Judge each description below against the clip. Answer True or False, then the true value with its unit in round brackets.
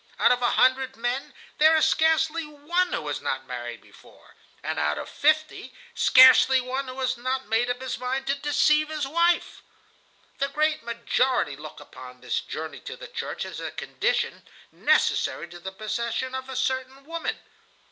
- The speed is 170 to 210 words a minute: True (175 wpm)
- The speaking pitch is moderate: False (260 Hz)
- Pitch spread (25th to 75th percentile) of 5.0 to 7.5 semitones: False (4.3 semitones)